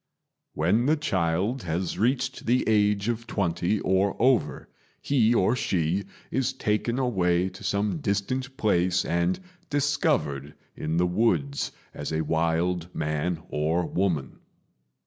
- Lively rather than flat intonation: Yes, wide, 5.7 semitones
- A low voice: Yes, very low, 95 Hz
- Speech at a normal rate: No, slow, 125 wpm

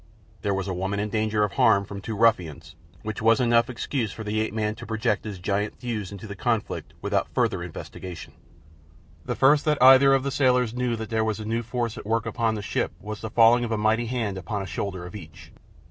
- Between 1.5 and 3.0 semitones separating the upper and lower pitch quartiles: Yes, narrow, 2.6 semitones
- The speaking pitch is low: Yes, low, 110 Hz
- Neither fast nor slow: No, fast, 230 wpm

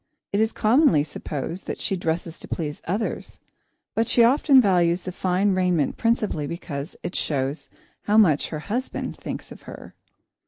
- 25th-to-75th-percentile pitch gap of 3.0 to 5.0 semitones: No, wide, 5.4 semitones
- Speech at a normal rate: Yes, average, 155 wpm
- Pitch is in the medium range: Yes, medium, 180 Hz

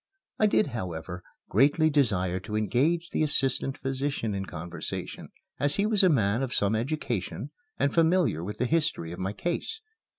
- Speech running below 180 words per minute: Yes, average, 165 wpm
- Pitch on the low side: Yes, low, 130 Hz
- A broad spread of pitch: Yes, wide, 7.8 semitones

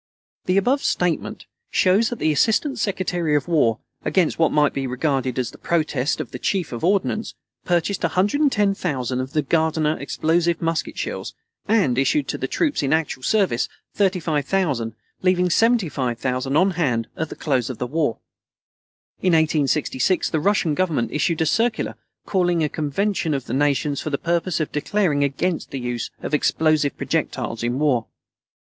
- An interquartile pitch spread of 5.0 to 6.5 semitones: Yes, average, 5.3 semitones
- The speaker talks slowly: No, average, 160 wpm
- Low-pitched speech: No, medium, 160 Hz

